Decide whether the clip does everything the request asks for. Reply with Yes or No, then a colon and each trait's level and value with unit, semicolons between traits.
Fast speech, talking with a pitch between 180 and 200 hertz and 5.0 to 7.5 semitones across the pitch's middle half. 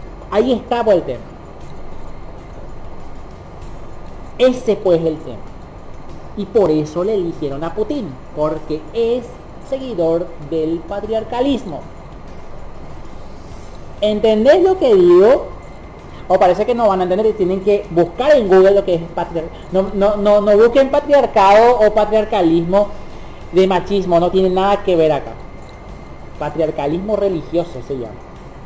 No: average, 135 wpm; high, 190 Hz; wide, 5.5 semitones